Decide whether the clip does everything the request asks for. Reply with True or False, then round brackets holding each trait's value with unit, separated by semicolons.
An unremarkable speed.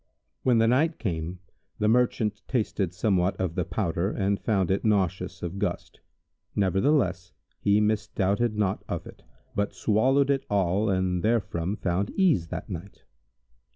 True (145 wpm)